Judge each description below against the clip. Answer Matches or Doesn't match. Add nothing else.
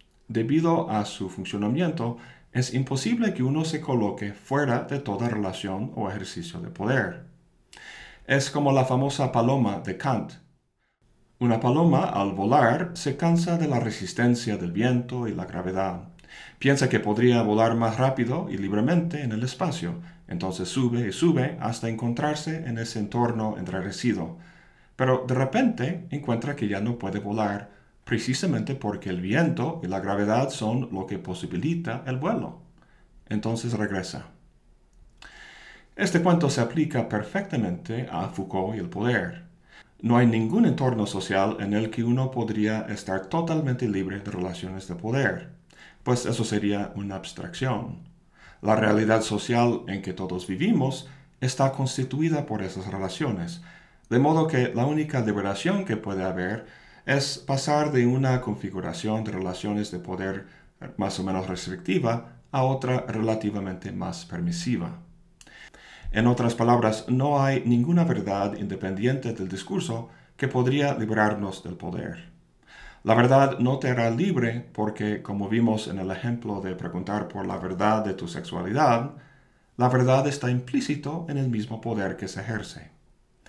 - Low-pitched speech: Matches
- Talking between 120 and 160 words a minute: Matches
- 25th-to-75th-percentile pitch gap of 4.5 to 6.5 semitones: Matches